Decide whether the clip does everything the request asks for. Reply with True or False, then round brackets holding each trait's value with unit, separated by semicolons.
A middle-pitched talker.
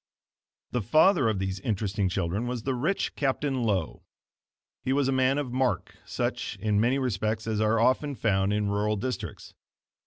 False (115 Hz)